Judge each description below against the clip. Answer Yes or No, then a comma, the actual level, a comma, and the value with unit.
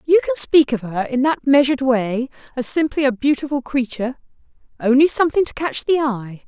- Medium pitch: No, very high, 265 Hz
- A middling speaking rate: Yes, average, 175 wpm